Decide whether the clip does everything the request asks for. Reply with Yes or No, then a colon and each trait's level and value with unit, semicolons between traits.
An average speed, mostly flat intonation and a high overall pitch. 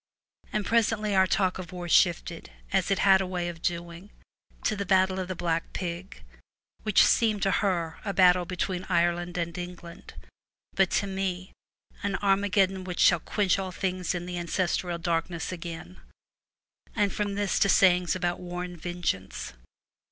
No: average, 165 wpm; narrow, 1.9 semitones; medium, 180 Hz